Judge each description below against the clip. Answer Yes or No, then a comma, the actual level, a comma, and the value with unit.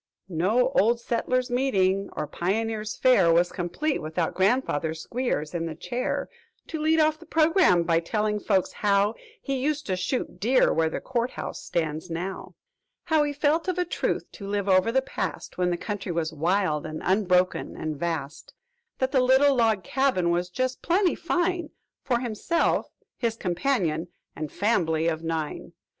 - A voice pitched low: No, high, 205 Hz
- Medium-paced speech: Yes, average, 165 wpm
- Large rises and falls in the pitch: Yes, wide, 7.2 semitones